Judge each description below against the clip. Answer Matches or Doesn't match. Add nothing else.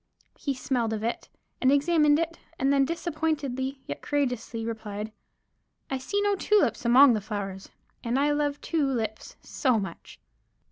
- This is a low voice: Doesn't match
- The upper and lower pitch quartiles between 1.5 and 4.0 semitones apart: Doesn't match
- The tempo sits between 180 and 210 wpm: Doesn't match